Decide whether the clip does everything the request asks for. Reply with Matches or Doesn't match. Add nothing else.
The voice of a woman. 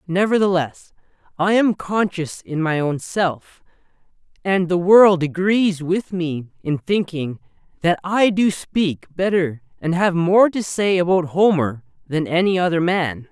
Doesn't match